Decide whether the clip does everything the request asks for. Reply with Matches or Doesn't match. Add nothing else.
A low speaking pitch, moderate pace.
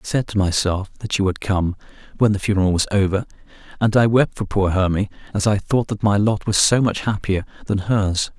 Doesn't match